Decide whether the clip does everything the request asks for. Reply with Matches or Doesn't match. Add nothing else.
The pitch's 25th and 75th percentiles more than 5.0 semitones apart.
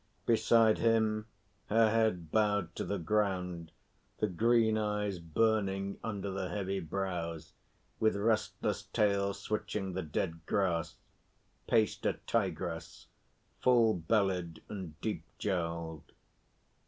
Doesn't match